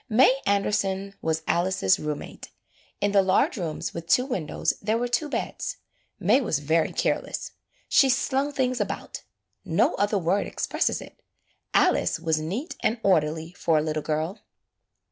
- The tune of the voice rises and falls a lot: Yes, wide, 6.8 semitones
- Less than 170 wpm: Yes, average, 155 wpm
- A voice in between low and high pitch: No, high, 195 Hz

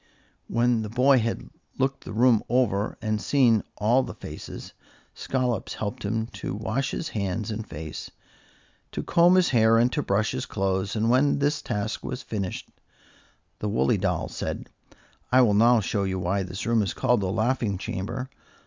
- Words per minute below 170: No, average, 175 wpm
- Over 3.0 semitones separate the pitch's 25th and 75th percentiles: Yes, average, 3.7 semitones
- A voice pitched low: Yes, low, 110 Hz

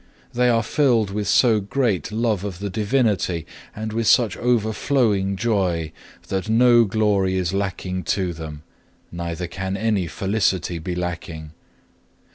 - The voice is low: Yes, low, 100 Hz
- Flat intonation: No, average, 3.7 semitones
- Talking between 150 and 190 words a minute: No, slow, 135 wpm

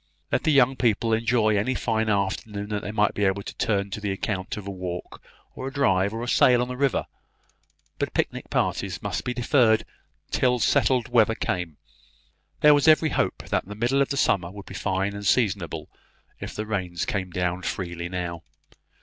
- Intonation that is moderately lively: Yes, average, 4.3 semitones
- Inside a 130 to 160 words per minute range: No, average, 195 wpm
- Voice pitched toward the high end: No, low, 105 Hz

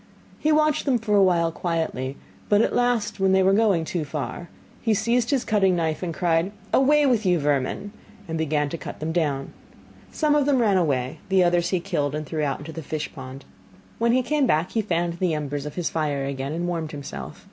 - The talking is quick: Yes, fast, 220 wpm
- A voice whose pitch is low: No, medium, 175 Hz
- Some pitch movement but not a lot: No, wide, 5.8 semitones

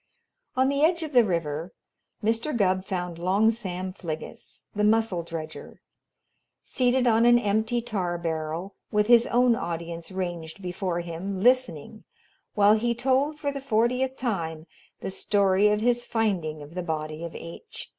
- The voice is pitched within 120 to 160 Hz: No, high, 200 Hz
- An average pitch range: No, wide, 5.9 semitones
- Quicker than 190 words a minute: No, average, 155 wpm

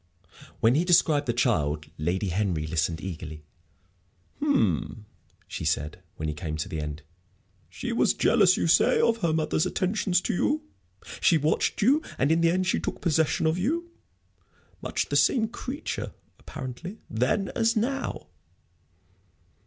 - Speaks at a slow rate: No, average, 150 wpm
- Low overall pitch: No, medium, 155 Hz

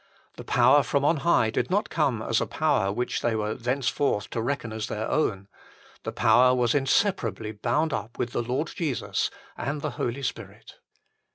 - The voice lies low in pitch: Yes, low, 125 Hz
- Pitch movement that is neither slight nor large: Yes, average, 4.1 semitones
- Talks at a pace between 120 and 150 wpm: No, average, 180 wpm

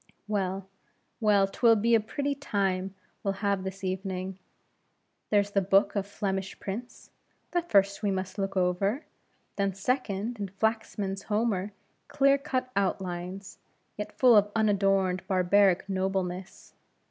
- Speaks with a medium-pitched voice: No, high, 200 Hz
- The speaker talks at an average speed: No, slow, 130 wpm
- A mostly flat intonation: Yes, narrow, 2.1 semitones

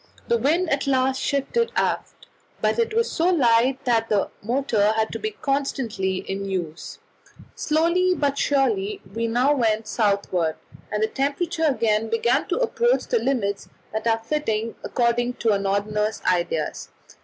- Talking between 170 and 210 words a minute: No, average, 155 wpm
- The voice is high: Yes, high, 235 Hz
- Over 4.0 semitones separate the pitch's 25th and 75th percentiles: Yes, average, 5.0 semitones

